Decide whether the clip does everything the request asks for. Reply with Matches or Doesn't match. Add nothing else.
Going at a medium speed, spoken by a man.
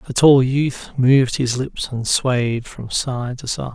Matches